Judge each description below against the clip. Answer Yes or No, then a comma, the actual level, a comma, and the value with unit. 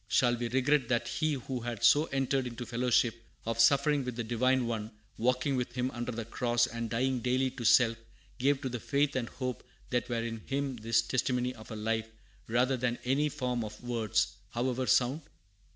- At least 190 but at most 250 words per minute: Yes, average, 195 wpm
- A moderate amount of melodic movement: No, narrow, 2.1 semitones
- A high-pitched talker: No, low, 125 Hz